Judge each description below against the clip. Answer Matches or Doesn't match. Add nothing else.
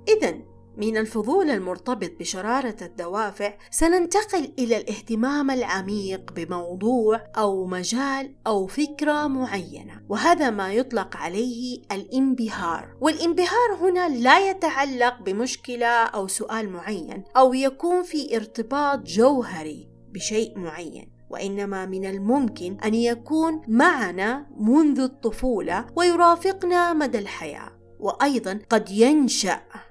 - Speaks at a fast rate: Doesn't match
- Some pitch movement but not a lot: Doesn't match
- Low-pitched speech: Doesn't match